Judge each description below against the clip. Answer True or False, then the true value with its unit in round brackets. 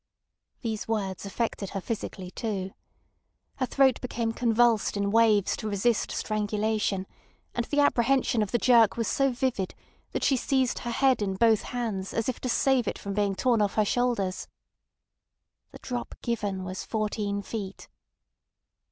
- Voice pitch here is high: True (220 Hz)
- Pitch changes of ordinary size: True (3.1 semitones)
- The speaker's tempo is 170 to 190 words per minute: False (155 wpm)